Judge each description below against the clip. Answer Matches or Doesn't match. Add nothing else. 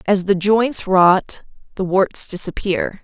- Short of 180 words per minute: Matches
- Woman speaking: Matches